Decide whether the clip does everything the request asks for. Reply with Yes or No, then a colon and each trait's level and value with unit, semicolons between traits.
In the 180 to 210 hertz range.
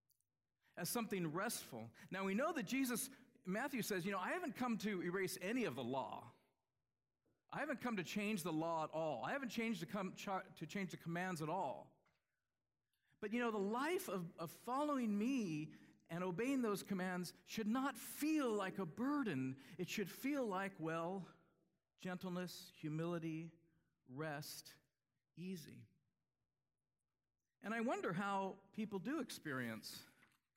Yes: high, 190 Hz